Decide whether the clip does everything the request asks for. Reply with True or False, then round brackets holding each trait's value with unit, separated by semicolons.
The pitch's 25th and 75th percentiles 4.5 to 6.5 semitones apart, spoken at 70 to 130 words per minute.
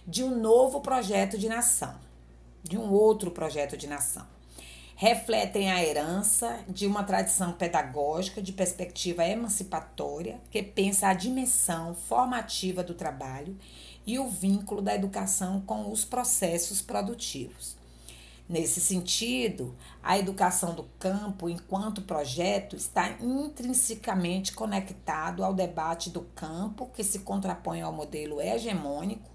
True (5.1 semitones; 120 wpm)